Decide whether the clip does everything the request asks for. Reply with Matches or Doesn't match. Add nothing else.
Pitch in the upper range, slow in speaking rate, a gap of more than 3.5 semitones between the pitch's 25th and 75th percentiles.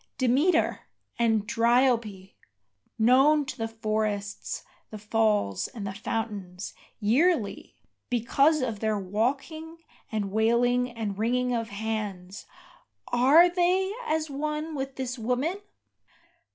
Matches